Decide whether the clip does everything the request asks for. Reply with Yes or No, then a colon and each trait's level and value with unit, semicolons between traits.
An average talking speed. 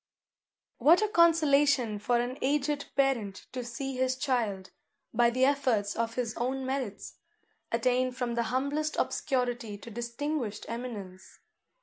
No: slow, 130 wpm